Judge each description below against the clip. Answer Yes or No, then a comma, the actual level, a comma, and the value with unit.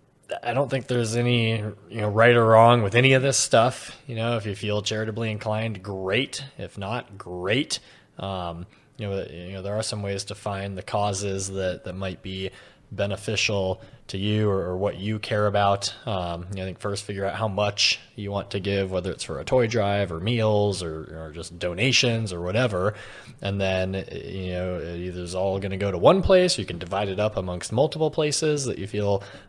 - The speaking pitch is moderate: No, low, 100 Hz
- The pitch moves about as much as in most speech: Yes, average, 3.0 semitones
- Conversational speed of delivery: No, fast, 215 wpm